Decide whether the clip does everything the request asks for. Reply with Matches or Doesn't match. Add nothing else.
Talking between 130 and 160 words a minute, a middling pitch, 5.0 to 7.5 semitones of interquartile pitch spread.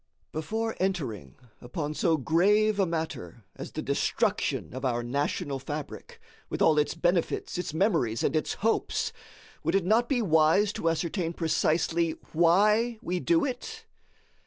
Matches